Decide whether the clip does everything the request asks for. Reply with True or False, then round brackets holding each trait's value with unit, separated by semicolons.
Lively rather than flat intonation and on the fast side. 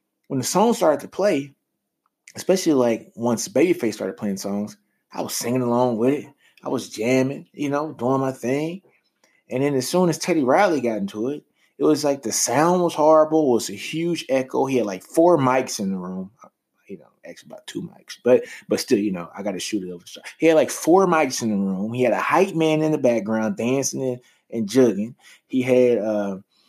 True (5.7 semitones; 220 wpm)